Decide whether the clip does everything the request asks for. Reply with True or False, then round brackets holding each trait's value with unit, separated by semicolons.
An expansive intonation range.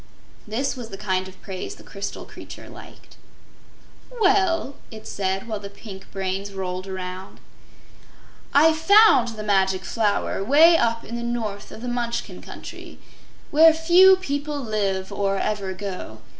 True (6.7 semitones)